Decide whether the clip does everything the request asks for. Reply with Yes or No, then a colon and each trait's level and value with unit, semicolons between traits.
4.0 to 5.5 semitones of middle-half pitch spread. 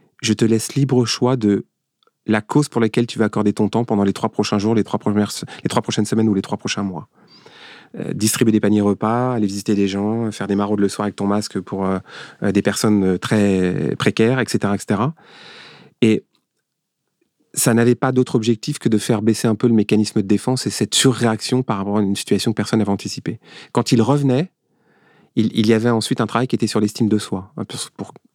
No: average, 2.7 semitones